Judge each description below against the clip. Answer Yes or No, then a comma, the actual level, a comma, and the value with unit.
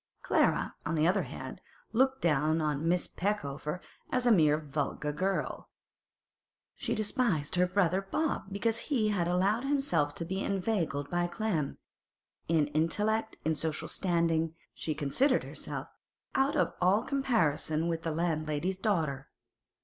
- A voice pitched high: No, medium, 175 Hz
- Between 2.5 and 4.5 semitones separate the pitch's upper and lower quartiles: No, wide, 5.4 semitones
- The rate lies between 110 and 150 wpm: Yes, average, 140 wpm